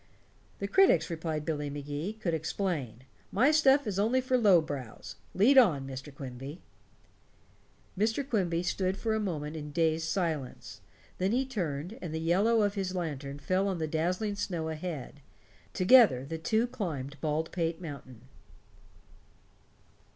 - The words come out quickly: No, average, 145 wpm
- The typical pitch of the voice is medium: Yes, medium, 170 Hz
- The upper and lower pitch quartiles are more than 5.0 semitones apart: Yes, wide, 5.5 semitones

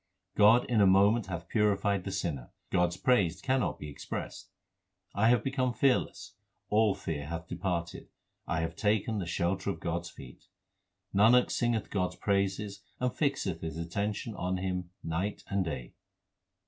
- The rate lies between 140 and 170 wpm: Yes, average, 160 wpm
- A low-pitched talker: Yes, very low, 95 Hz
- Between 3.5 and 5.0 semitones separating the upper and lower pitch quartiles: Yes, average, 3.9 semitones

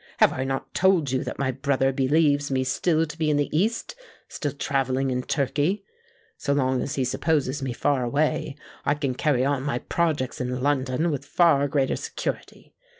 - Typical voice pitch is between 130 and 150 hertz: Yes, medium, 140 Hz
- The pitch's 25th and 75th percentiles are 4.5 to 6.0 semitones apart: No, narrow, 2.6 semitones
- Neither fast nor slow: Yes, average, 180 wpm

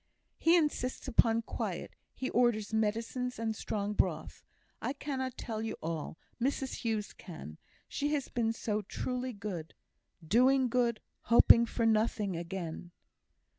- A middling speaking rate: No, slow, 130 wpm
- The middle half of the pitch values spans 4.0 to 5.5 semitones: No, average, 3.4 semitones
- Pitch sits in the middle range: No, high, 225 Hz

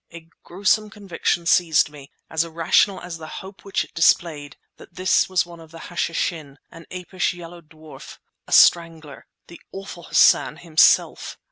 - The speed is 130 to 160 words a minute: Yes, average, 150 wpm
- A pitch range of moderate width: No, narrow, 2.1 semitones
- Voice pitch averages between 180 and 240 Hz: No, medium, 170 Hz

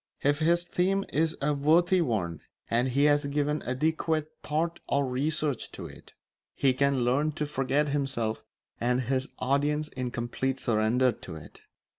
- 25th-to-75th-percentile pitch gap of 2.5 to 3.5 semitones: Yes, average, 3.2 semitones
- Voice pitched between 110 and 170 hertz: Yes, medium, 140 Hz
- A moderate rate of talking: Yes, average, 155 wpm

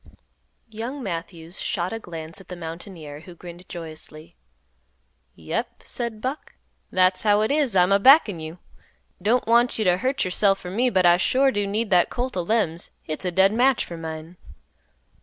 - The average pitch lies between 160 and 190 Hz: Yes, medium, 185 Hz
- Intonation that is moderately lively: Yes, average, 4.8 semitones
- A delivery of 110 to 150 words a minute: No, average, 175 wpm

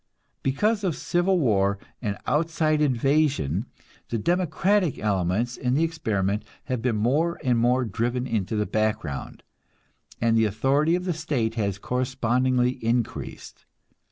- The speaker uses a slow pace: Yes, slow, 130 wpm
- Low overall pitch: Yes, low, 125 Hz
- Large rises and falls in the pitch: Yes, wide, 5.9 semitones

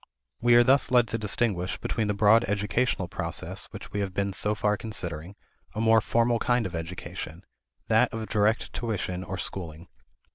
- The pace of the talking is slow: No, average, 175 wpm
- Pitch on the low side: Yes, low, 105 Hz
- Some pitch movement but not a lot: Yes, average, 3.4 semitones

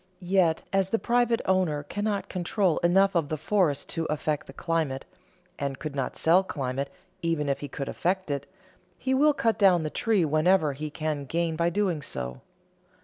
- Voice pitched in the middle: Yes, medium, 165 Hz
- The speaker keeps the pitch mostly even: No, average, 4.7 semitones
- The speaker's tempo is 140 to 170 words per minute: No, average, 180 wpm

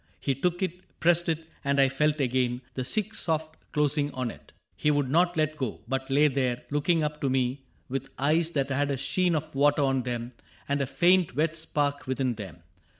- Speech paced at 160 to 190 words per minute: No, fast, 205 wpm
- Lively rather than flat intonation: No, average, 3.1 semitones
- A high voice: No, medium, 145 Hz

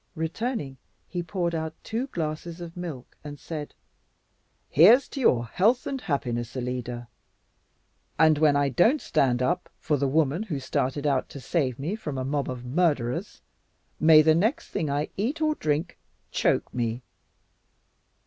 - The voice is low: No, medium, 155 Hz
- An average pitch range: Yes, average, 4.9 semitones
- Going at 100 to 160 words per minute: Yes, average, 155 wpm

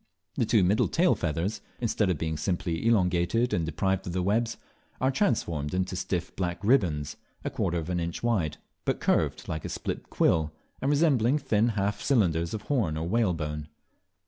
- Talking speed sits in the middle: Yes, average, 175 wpm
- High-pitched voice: No, very low, 90 Hz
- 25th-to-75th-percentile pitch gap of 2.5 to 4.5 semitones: No, wide, 5.6 semitones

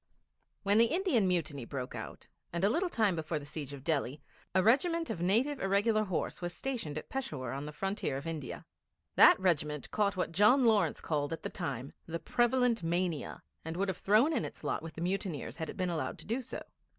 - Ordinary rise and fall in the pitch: No, wide, 6.3 semitones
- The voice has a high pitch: No, medium, 180 Hz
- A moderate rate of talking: No, fast, 210 wpm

